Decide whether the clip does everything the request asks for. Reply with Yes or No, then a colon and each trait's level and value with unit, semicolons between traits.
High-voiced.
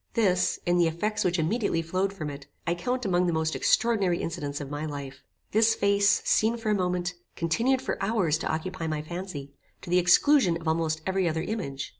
No: medium, 175 Hz